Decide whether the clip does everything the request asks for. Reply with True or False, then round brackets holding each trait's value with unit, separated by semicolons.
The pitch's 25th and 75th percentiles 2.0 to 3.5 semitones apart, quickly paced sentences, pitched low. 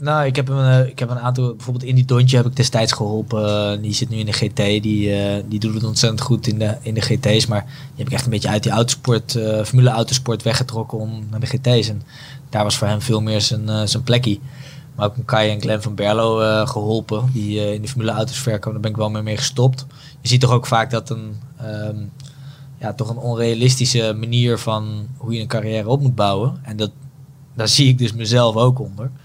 True (2.9 semitones; 235 wpm; 115 Hz)